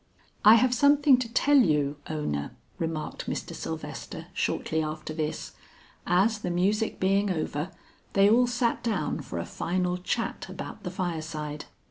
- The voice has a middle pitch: Yes, medium, 180 Hz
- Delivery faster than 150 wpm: No, average, 145 wpm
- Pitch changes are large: Yes, wide, 6.5 semitones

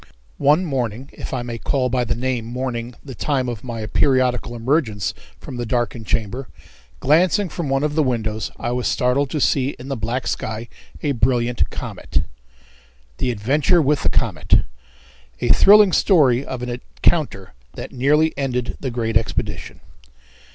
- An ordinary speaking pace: Yes, average, 160 wpm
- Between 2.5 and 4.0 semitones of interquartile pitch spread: Yes, average, 3.0 semitones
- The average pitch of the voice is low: Yes, low, 125 Hz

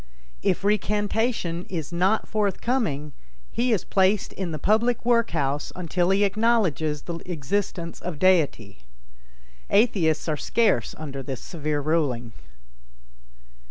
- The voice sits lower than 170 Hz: No, medium, 180 Hz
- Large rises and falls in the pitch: Yes, wide, 5.7 semitones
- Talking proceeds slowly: Yes, slow, 120 wpm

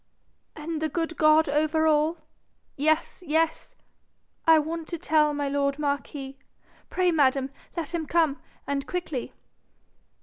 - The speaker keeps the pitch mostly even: Yes, narrow, 2.3 semitones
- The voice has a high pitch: Yes, very high, 310 Hz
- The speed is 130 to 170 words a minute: Yes, slow, 135 wpm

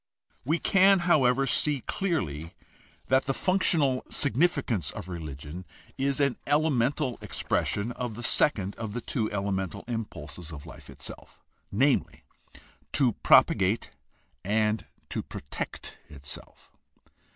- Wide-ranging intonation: Yes, wide, 6.9 semitones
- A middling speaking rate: No, slow, 115 wpm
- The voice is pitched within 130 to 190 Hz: No, low, 120 Hz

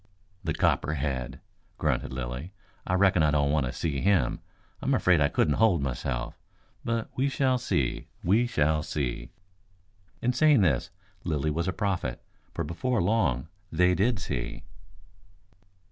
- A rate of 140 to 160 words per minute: Yes, average, 145 wpm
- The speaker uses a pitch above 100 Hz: No, very low, 85 Hz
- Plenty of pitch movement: Yes, wide, 6.4 semitones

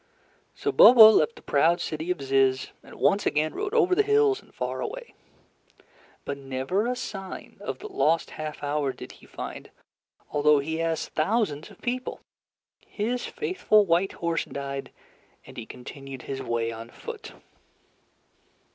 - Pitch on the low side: No, medium, 165 Hz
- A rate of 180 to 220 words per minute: No, average, 155 wpm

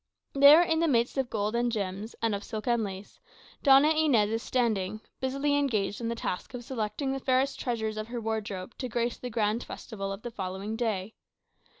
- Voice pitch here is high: Yes, high, 230 Hz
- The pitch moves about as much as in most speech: Yes, average, 3.6 semitones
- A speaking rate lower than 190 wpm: No, average, 200 wpm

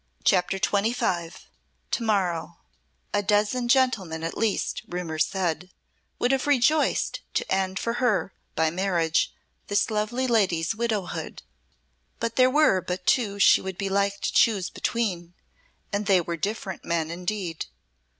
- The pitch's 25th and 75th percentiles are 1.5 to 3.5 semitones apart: No, average, 4.3 semitones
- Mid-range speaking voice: No, high, 195 Hz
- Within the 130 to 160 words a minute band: Yes, average, 140 wpm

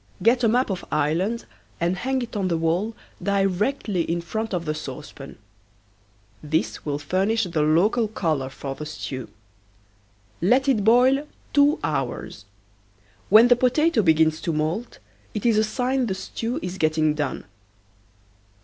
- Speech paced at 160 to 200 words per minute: No, average, 150 wpm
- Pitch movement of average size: No, wide, 6.9 semitones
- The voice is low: No, high, 190 Hz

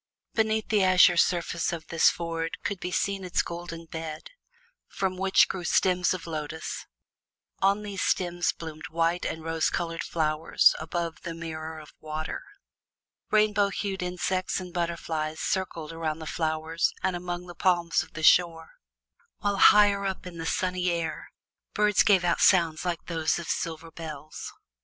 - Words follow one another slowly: No, average, 155 wpm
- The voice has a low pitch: No, medium, 170 Hz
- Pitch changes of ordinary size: No, narrow, 2.3 semitones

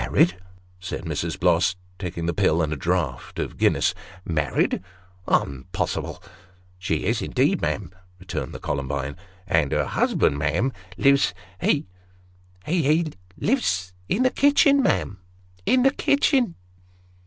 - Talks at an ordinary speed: Yes, average, 155 wpm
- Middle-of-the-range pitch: No, very low, 90 Hz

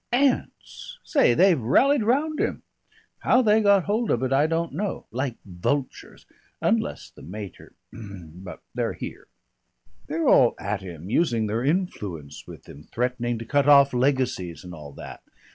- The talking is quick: No, average, 155 wpm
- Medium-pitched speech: No, low, 130 Hz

